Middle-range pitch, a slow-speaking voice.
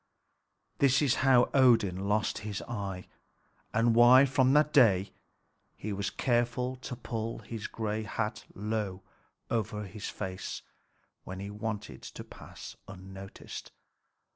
No: low, 110 Hz; slow, 125 wpm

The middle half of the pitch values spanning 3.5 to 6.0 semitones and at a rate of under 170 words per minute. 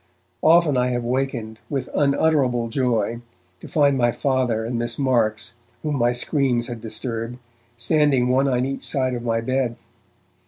No: narrow, 2.6 semitones; average, 155 wpm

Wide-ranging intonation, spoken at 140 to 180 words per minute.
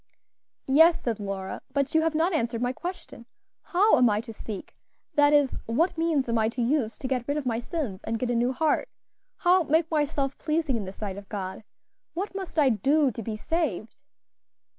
No: wide, 5.8 semitones; fast, 205 wpm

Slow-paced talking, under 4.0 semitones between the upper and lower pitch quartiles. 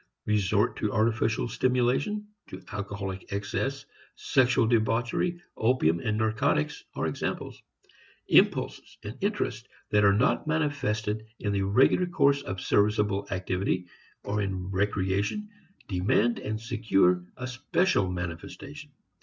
No: slow, 115 wpm; average, 4.7 semitones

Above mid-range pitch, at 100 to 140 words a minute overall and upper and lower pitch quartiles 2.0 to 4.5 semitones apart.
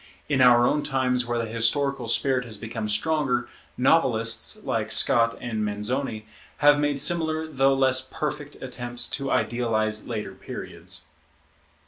No: low, 125 Hz; slow, 135 wpm; average, 3.6 semitones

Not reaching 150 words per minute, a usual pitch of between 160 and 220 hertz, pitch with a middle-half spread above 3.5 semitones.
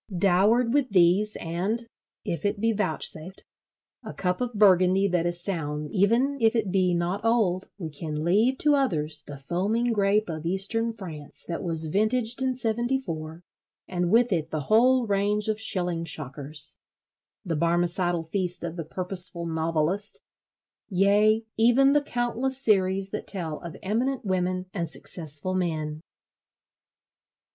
Yes: average, 140 wpm; high, 190 Hz; average, 4.7 semitones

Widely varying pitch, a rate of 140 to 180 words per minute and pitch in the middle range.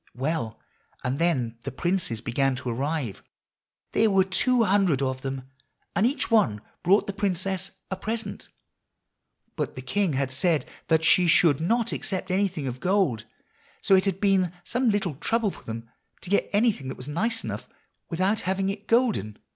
Yes: wide, 7.0 semitones; average, 170 wpm; medium, 180 Hz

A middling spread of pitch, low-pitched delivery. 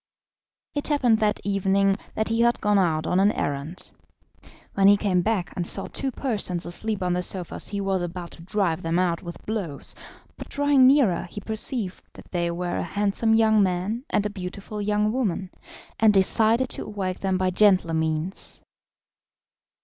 No: average, 3.4 semitones; high, 195 Hz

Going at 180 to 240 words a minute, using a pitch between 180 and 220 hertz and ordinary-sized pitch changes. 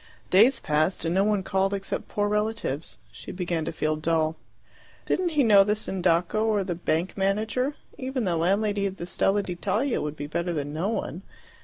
Yes: average, 185 wpm; high, 190 Hz; average, 4.2 semitones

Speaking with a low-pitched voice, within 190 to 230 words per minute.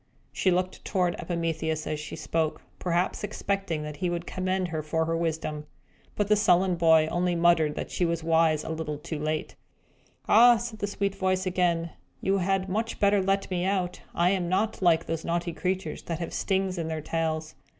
No: medium, 175 Hz; average, 195 wpm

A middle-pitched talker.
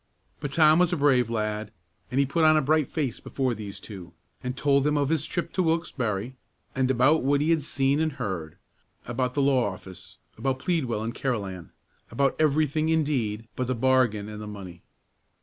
No: low, 130 Hz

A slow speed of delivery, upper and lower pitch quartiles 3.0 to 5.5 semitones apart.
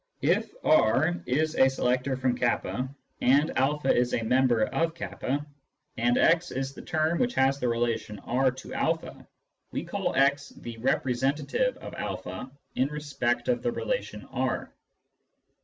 No: average, 155 wpm; average, 3.6 semitones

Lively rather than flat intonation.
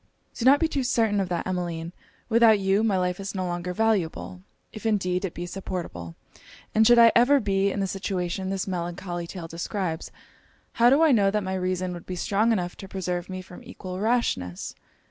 No: average, 3.3 semitones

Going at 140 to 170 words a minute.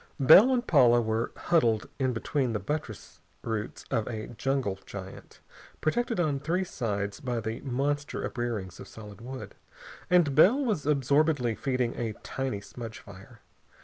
Yes: average, 145 wpm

